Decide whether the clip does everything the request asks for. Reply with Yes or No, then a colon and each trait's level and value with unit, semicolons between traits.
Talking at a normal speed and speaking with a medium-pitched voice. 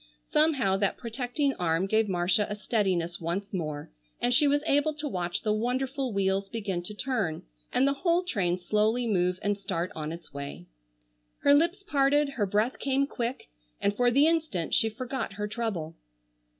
No: average, 175 wpm; high, 215 Hz